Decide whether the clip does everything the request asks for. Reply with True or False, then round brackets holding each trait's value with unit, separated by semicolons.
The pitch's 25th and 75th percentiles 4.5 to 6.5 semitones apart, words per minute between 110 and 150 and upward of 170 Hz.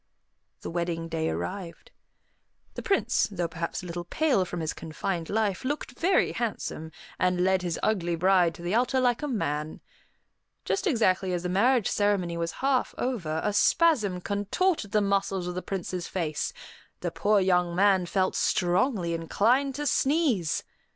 False (5.2 semitones; 160 wpm; 190 Hz)